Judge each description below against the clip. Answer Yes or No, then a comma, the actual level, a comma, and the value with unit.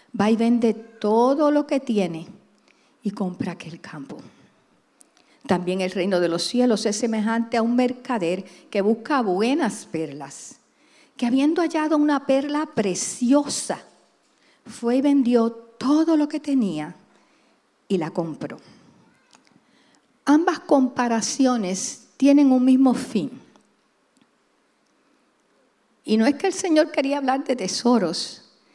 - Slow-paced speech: Yes, slow, 120 wpm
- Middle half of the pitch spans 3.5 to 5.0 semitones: No, wide, 5.5 semitones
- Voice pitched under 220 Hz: No, high, 240 Hz